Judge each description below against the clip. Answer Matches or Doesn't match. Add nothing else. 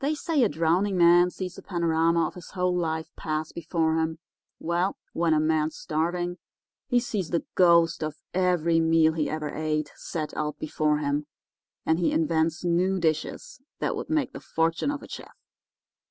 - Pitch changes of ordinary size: Doesn't match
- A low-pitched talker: Doesn't match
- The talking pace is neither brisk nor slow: Matches